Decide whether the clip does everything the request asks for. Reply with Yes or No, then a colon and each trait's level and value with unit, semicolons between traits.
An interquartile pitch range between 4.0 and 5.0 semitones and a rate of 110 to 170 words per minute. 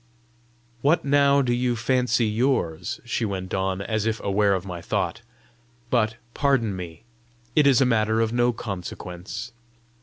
Yes: average, 4.5 semitones; average, 150 wpm